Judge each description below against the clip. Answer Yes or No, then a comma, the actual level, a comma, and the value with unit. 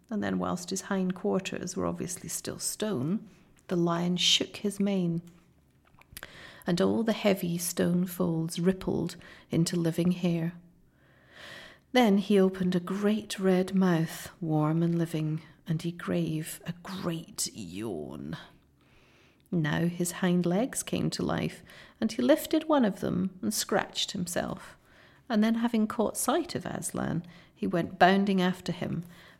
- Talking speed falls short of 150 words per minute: Yes, average, 140 wpm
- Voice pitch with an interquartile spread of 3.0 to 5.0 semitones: No, narrow, 2.6 semitones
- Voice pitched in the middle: Yes, medium, 180 Hz